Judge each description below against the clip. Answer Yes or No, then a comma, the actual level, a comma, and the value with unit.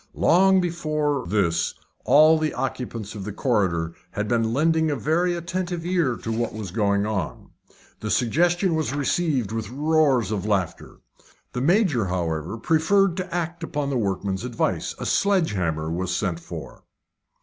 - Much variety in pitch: Yes, wide, 8.1 semitones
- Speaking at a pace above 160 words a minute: No, average, 155 wpm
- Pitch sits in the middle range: No, low, 125 Hz